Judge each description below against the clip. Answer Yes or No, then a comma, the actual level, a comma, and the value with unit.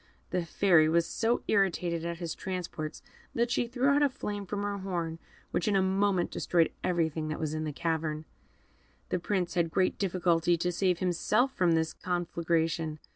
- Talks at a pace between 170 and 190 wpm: Yes, average, 180 wpm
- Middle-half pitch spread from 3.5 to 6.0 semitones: No, average, 3.0 semitones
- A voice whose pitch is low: No, medium, 175 Hz